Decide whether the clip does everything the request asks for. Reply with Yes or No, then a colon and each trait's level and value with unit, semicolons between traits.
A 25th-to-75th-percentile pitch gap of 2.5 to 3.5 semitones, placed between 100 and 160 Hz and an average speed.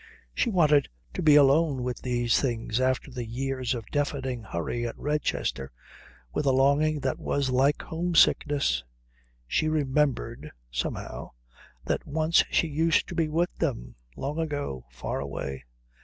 No: average, 4.1 semitones; low, 135 Hz; average, 145 wpm